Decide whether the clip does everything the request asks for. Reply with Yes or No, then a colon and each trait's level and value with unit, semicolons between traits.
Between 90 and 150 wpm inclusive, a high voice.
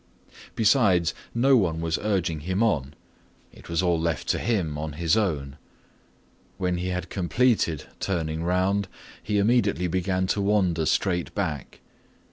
No: average, 140 wpm; very low, 90 Hz